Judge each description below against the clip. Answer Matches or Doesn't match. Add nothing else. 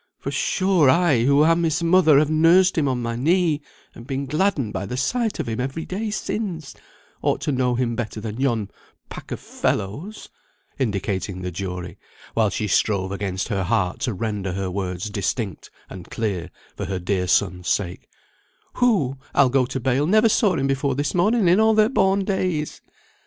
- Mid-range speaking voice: Doesn't match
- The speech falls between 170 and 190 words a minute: Matches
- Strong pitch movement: Matches